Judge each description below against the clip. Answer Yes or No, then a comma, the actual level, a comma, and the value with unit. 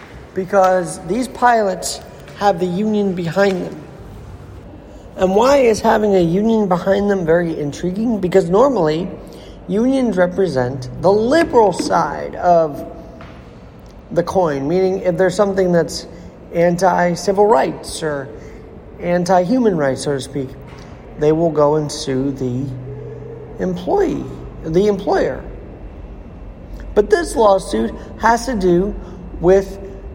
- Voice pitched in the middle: Yes, medium, 180 Hz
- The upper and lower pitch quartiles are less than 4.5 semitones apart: No, wide, 5.6 semitones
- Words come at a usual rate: No, slow, 115 wpm